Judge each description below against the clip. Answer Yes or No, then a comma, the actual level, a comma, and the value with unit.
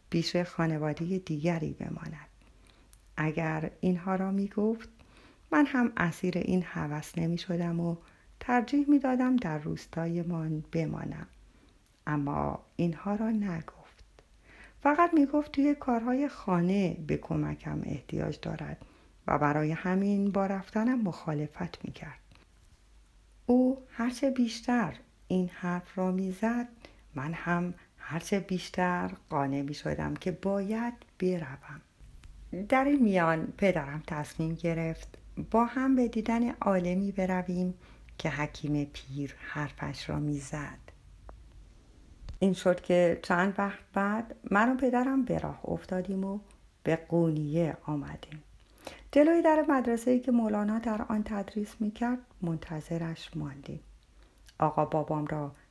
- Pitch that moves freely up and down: Yes, wide, 6.0 semitones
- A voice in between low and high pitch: Yes, medium, 180 Hz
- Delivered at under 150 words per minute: Yes, average, 125 wpm